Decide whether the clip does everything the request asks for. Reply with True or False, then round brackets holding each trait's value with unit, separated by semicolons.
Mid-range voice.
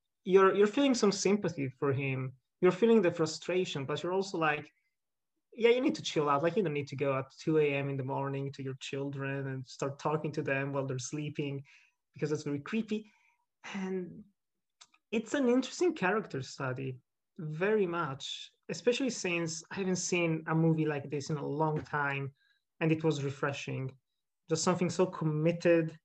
True (160 Hz)